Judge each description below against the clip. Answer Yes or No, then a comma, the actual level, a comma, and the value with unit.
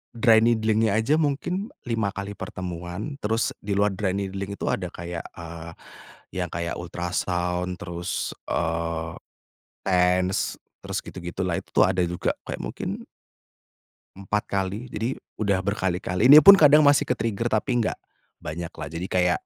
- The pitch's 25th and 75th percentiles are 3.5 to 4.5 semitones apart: Yes, average, 4.0 semitones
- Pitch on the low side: Yes, very low, 95 Hz